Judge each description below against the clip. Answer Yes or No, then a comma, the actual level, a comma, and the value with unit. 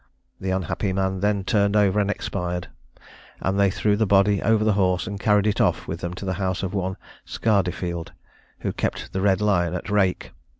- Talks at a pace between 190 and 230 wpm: Yes, average, 200 wpm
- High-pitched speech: No, very low, 95 Hz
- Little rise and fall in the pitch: Yes, narrow, 1.8 semitones